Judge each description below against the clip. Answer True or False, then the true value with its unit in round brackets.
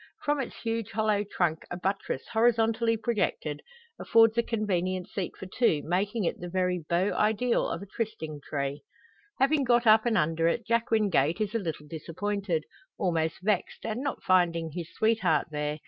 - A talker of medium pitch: False (200 Hz)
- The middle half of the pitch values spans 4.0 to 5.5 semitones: True (5.2 semitones)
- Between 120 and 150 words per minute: False (170 wpm)